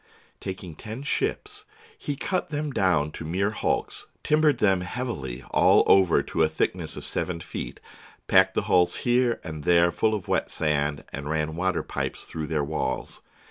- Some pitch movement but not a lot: No, wide, 7.4 semitones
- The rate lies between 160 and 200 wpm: Yes, average, 170 wpm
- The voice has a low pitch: Yes, very low, 90 Hz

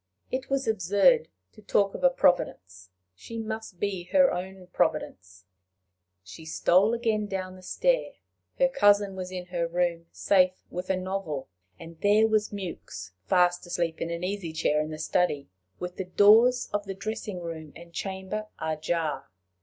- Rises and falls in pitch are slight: No, average, 3.7 semitones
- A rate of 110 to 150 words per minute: No, average, 165 wpm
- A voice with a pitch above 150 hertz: Yes, medium, 185 Hz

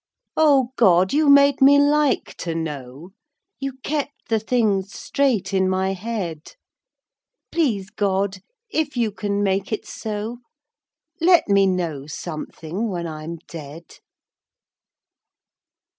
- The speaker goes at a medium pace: No, slow, 115 wpm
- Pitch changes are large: Yes, wide, 7.1 semitones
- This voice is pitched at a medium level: No, high, 200 Hz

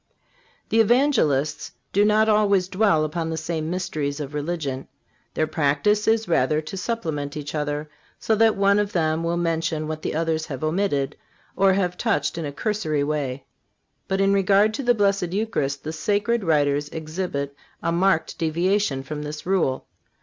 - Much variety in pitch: No, average, 5.0 semitones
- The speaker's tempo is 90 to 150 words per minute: No, average, 165 wpm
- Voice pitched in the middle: Yes, medium, 165 Hz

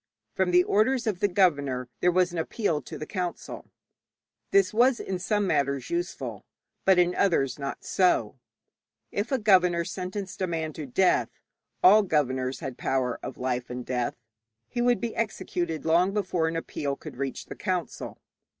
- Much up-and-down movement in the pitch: Yes, wide, 6.1 semitones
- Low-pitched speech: No, medium, 180 Hz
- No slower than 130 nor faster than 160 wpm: No, average, 170 wpm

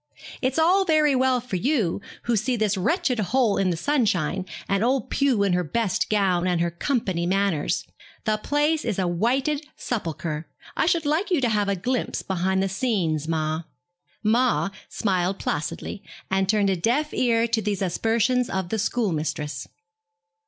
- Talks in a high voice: Yes, high, 210 Hz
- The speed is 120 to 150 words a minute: No, average, 165 wpm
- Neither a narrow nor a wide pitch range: No, wide, 5.9 semitones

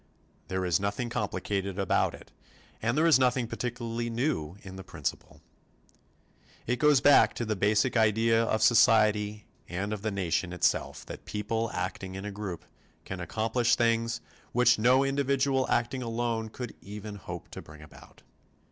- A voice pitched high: No, low, 110 Hz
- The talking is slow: No, average, 155 wpm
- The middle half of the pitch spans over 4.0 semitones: No, average, 3.5 semitones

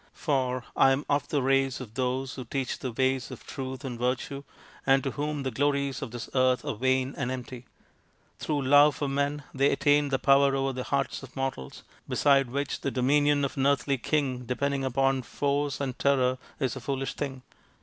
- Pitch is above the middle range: No, low, 135 Hz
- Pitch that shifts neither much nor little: No, narrow, 1.6 semitones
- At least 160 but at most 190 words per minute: No, average, 200 wpm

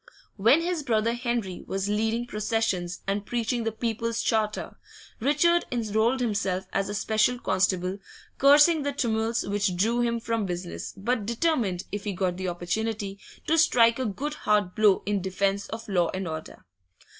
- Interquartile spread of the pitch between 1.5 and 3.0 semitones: No, average, 3.5 semitones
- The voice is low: No, high, 220 Hz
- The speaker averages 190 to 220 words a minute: No, average, 160 wpm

